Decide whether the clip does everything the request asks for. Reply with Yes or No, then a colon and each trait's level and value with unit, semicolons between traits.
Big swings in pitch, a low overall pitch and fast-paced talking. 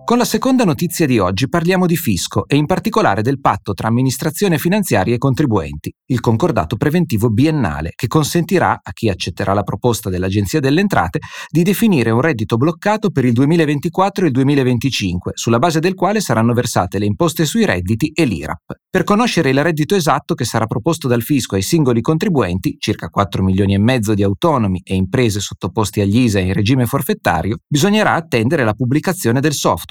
Yes: wide, 7.8 semitones; low, 130 Hz; fast, 180 wpm